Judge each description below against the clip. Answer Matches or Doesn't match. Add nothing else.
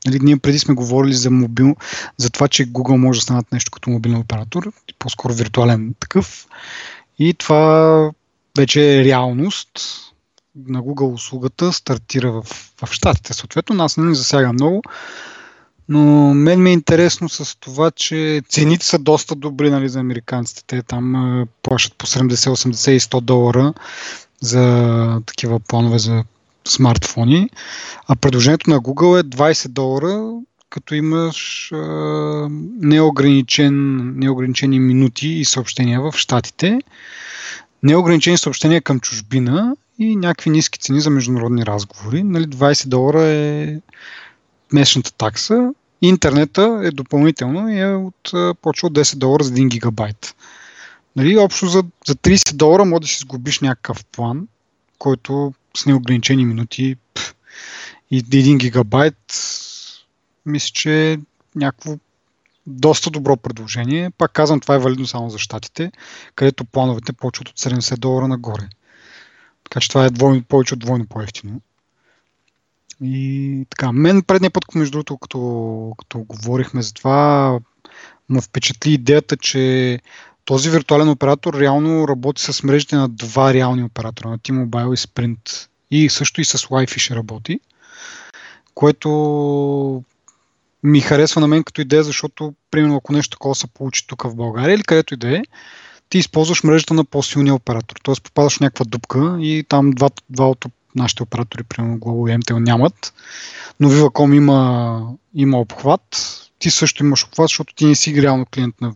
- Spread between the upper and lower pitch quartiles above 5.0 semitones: Doesn't match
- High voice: Doesn't match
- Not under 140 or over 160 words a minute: Matches